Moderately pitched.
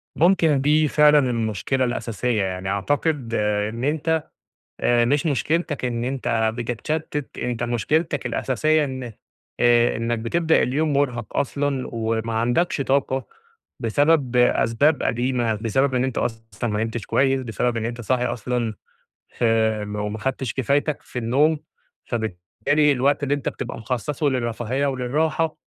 No: low, 125 Hz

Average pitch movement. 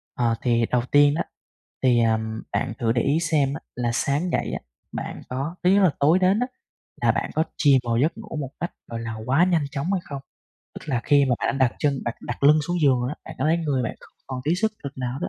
Yes: average, 4.6 semitones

